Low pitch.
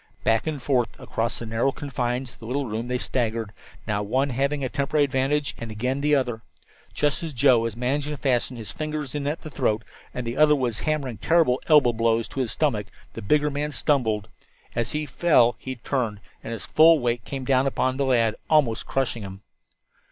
Yes: low, 130 Hz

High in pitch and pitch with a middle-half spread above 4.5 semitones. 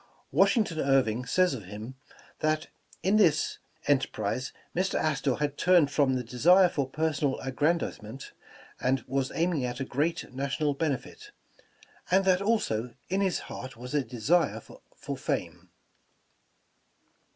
No: medium, 145 Hz; average, 5.0 semitones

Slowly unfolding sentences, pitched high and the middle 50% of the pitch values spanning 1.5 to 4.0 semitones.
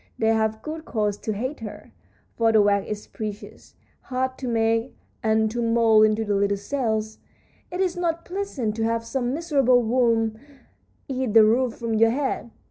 No: average, 175 wpm; high, 230 Hz; average, 3.0 semitones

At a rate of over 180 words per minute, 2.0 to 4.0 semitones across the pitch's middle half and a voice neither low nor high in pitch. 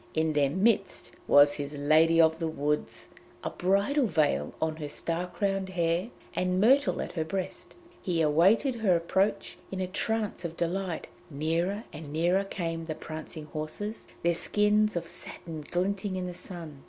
No: average, 165 wpm; average, 3.7 semitones; medium, 170 Hz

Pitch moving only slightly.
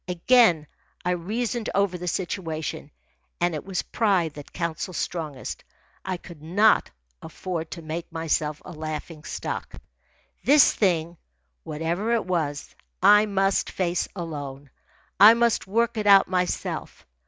No: average, 4.0 semitones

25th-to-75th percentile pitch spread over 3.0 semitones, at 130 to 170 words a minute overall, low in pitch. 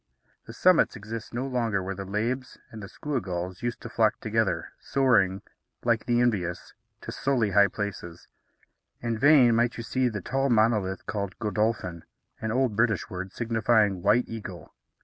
Yes: average, 3.5 semitones; average, 165 wpm; low, 110 Hz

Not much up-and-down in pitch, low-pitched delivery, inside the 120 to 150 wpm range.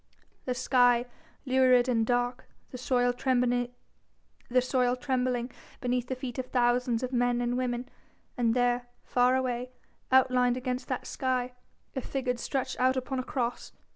No: narrow, 0.8 semitones; very high, 250 Hz; average, 140 wpm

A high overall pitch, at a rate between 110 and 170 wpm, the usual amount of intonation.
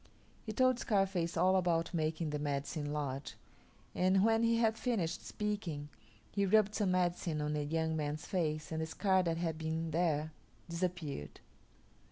No: medium, 165 Hz; average, 160 wpm; average, 3.9 semitones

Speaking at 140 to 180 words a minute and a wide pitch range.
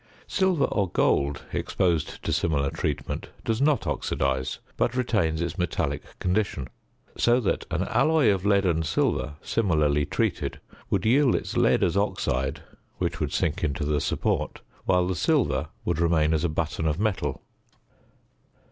Yes: average, 150 wpm; wide, 5.7 semitones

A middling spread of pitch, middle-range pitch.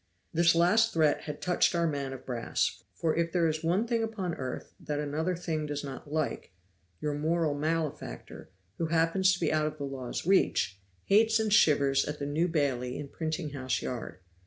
Yes: average, 3.1 semitones; medium, 155 Hz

